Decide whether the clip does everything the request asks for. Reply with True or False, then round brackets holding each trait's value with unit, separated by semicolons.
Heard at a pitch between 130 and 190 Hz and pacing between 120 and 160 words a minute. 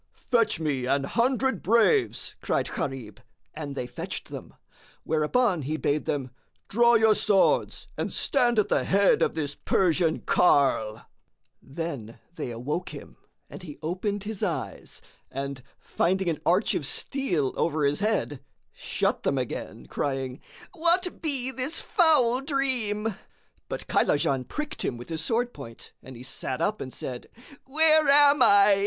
True (185 Hz; 150 wpm)